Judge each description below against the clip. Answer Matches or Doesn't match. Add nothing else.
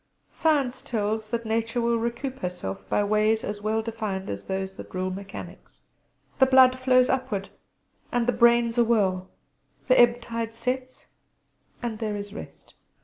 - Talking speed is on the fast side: Doesn't match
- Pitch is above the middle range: Matches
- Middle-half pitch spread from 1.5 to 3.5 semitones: Matches